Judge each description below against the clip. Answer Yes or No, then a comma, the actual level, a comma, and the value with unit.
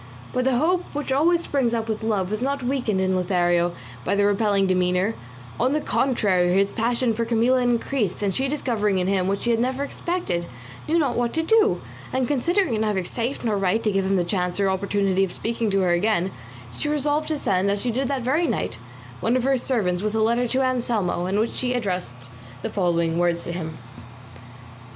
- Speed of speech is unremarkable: No, fast, 210 wpm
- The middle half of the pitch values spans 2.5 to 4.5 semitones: No, wide, 5.4 semitones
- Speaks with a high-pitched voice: Yes, high, 220 Hz